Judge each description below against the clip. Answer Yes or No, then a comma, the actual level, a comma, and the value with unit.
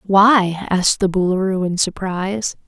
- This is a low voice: No, high, 190 Hz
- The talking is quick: No, slow, 135 wpm